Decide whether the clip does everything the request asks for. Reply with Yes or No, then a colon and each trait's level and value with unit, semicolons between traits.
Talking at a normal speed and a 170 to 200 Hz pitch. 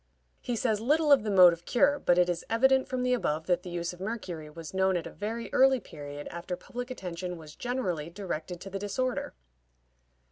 No: fast, 210 wpm; high, 190 Hz